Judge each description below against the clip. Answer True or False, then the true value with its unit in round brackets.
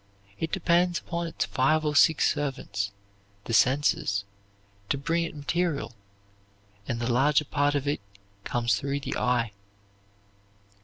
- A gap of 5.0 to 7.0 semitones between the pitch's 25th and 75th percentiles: False (4.5 semitones)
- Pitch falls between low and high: True (145 Hz)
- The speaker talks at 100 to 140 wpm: True (135 wpm)